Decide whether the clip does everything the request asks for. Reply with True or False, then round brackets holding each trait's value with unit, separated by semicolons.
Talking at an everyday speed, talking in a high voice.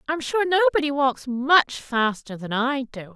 True (170 wpm; 275 Hz)